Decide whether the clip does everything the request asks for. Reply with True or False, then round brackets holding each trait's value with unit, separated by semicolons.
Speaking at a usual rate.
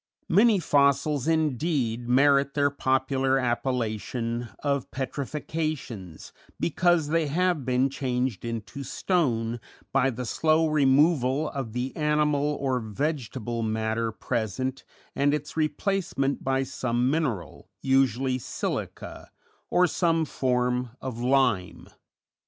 False (105 wpm)